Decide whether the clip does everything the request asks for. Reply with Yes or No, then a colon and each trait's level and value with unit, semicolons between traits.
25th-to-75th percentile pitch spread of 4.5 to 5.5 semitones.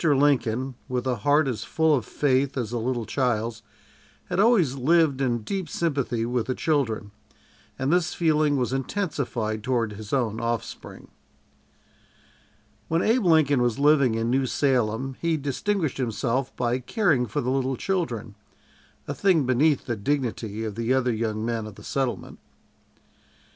No: average, 4.0 semitones